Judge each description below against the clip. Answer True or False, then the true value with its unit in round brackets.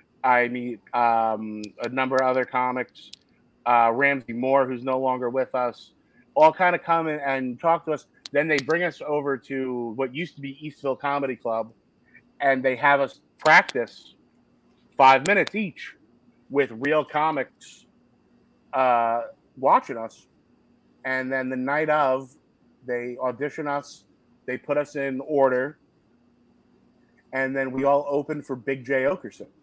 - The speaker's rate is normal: True (150 wpm)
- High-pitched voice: False (135 Hz)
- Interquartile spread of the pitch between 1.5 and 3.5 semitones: True (2.5 semitones)